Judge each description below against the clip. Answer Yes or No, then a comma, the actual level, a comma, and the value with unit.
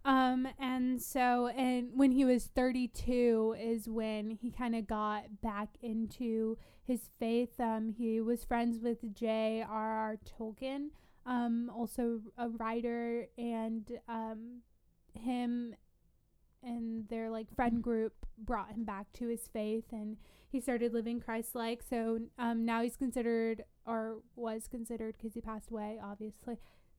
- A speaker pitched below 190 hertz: No, high, 230 Hz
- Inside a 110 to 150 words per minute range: Yes, average, 140 wpm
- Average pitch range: No, narrow, 1.5 semitones